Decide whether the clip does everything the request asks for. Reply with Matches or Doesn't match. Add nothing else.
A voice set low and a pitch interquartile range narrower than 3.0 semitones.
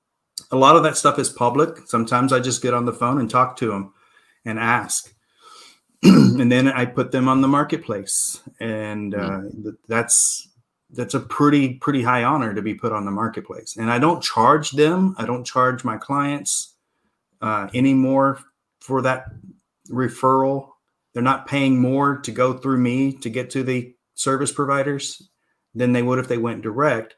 Matches